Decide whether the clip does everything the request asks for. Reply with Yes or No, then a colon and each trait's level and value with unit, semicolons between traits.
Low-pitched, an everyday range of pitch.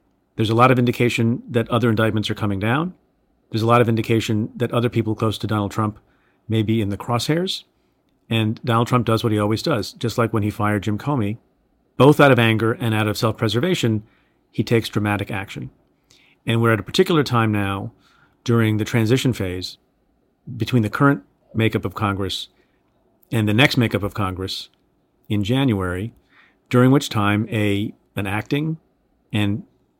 No: low, 110 Hz; narrow, 2.3 semitones